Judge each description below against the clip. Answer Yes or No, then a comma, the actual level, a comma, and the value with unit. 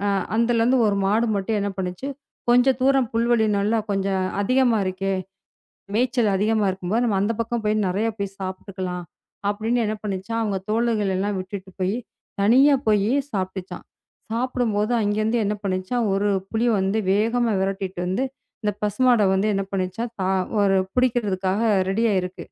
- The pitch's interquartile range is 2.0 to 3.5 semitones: Yes, average, 3.2 semitones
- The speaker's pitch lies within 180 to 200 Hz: No, high, 210 Hz